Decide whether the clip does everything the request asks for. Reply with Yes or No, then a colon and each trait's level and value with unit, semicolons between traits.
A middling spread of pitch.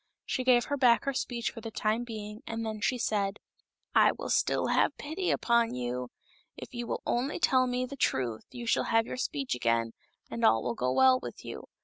Yes: average, 4.4 semitones